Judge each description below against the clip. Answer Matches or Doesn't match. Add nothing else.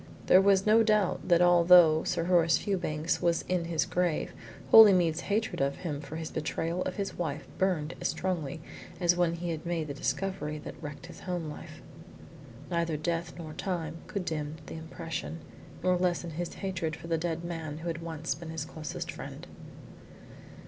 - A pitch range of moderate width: Doesn't match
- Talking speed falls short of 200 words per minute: Matches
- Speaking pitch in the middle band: Matches